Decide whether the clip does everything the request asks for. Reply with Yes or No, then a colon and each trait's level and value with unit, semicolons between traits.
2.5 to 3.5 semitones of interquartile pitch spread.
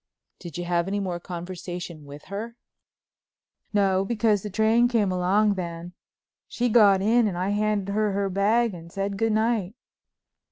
Yes: average, 3.2 semitones